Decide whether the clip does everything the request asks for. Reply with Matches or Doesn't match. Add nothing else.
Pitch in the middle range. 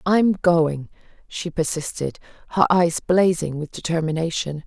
Matches